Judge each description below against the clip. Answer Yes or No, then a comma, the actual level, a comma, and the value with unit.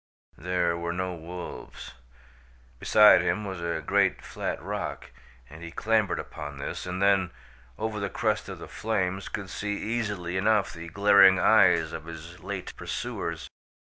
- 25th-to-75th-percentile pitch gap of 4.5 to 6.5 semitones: No, average, 3.1 semitones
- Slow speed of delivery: No, average, 150 wpm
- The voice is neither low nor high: No, very low, 95 Hz